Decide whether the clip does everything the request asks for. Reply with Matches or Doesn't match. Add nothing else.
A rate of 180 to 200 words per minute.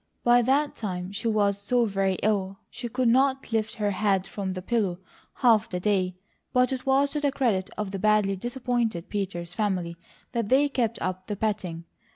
Matches